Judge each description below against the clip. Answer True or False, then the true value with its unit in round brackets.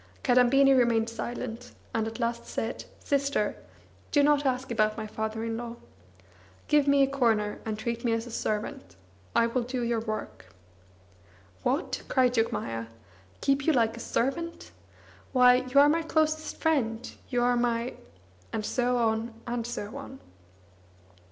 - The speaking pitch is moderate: False (240 Hz)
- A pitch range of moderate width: True (3.2 semitones)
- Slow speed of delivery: False (155 wpm)